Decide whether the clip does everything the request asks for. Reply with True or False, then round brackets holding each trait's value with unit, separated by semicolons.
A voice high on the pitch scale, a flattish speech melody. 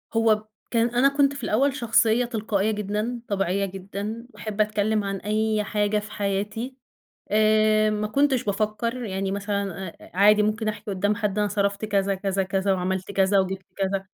True (210 Hz; 1.8 semitones)